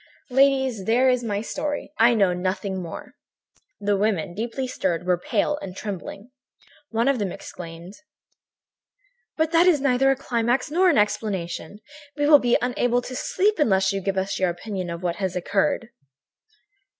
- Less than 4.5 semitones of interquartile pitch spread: No, wide, 5.6 semitones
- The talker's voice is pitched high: Yes, high, 220 Hz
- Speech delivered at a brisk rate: No, average, 160 wpm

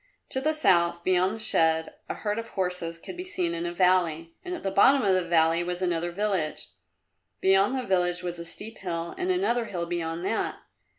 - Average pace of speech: No, fast, 210 wpm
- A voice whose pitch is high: No, medium, 180 Hz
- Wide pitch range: No, average, 3.8 semitones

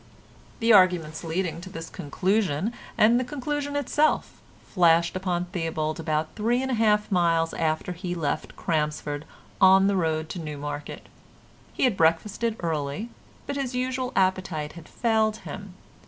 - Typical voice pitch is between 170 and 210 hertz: Yes, medium, 185 Hz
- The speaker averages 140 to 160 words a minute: Yes, average, 150 wpm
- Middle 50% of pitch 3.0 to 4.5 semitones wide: No, wide, 5.5 semitones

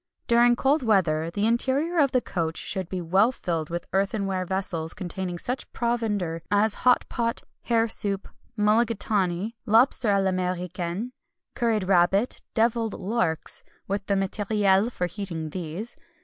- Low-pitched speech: No, high, 200 Hz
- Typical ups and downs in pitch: Yes, average, 4.2 semitones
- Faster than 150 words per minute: No, slow, 135 wpm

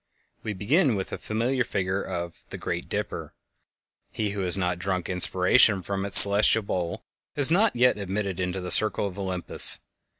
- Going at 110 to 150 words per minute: No, average, 170 wpm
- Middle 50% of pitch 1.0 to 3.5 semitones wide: Yes, average, 2.9 semitones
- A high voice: No, low, 100 Hz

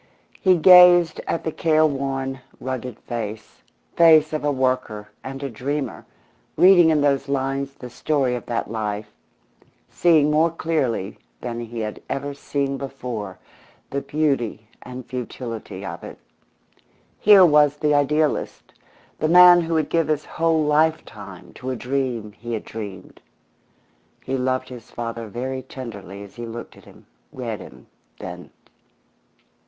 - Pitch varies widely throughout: No, average, 4.6 semitones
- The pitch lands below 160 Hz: Yes, low, 135 Hz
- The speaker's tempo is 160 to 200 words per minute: No, average, 145 wpm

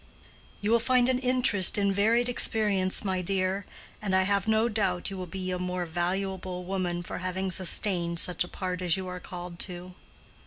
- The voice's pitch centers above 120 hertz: Yes, high, 190 Hz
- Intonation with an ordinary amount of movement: No, narrow, 2.1 semitones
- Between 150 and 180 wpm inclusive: No, average, 190 wpm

